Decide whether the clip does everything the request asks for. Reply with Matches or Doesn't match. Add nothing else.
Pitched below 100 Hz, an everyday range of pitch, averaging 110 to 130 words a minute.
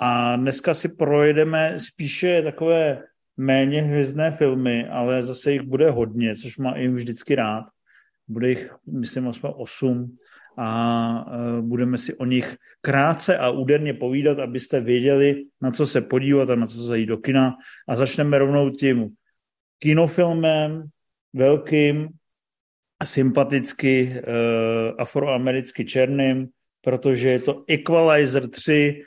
Doesn't match